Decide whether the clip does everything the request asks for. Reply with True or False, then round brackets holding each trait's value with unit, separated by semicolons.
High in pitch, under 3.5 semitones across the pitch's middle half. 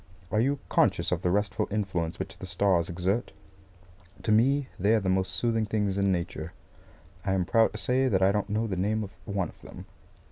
False (100 Hz; 2.7 semitones)